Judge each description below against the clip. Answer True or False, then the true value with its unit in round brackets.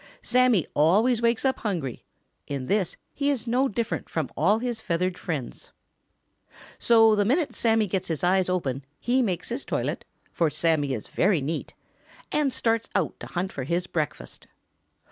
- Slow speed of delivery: False (165 wpm)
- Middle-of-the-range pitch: False (195 Hz)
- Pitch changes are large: True (6.1 semitones)